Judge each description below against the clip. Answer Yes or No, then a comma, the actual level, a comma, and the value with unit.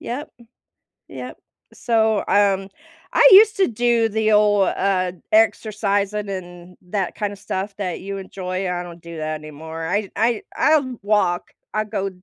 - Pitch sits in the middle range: No, high, 200 Hz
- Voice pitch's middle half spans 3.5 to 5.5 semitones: No, average, 3.1 semitones